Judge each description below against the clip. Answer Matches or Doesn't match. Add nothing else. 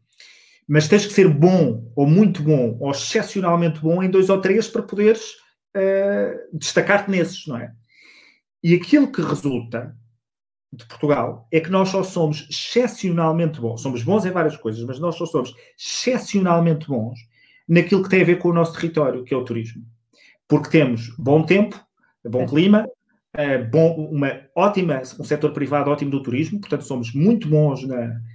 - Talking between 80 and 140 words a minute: Doesn't match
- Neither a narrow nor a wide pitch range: Doesn't match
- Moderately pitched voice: Matches